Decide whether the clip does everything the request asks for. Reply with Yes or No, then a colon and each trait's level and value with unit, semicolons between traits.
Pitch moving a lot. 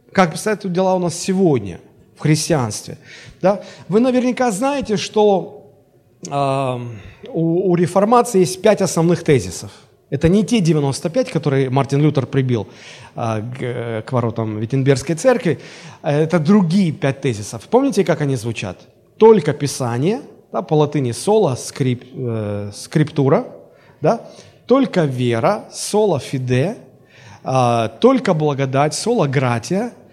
Yes: wide, 7.0 semitones